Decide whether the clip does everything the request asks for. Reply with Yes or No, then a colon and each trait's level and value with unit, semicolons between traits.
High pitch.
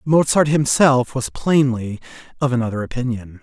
No: low, 130 Hz